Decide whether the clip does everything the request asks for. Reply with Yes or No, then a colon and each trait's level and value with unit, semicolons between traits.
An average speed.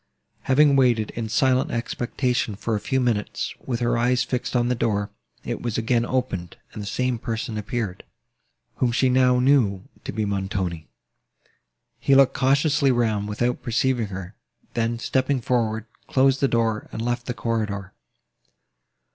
Yes: average, 155 wpm